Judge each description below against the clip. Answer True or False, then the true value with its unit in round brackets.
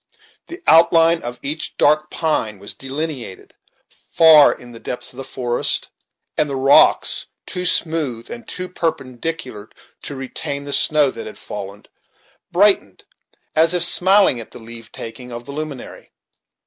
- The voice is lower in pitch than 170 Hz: True (140 Hz)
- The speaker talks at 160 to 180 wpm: False (150 wpm)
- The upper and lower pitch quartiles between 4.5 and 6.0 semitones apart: True (5.3 semitones)